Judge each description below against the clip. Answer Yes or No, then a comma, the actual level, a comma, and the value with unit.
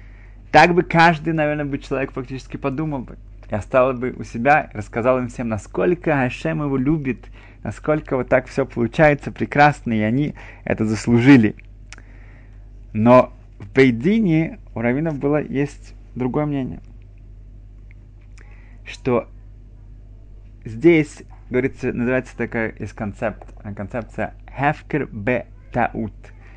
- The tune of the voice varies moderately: Yes, average, 4.5 semitones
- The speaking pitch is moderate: No, low, 115 Hz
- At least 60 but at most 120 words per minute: Yes, average, 115 wpm